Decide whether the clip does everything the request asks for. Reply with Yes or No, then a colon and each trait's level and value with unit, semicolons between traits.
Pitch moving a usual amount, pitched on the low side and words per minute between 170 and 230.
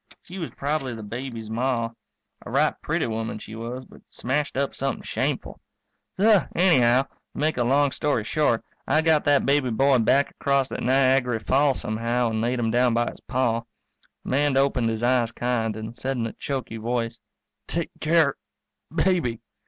Yes: average, 3.3 semitones; low, 125 Hz; average, 175 wpm